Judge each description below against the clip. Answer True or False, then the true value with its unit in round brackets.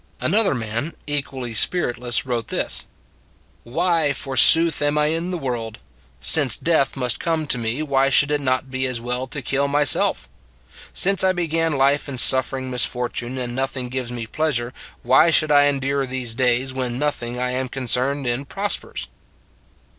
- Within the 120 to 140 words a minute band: False (170 wpm)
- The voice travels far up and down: False (3.1 semitones)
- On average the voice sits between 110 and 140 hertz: True (135 Hz)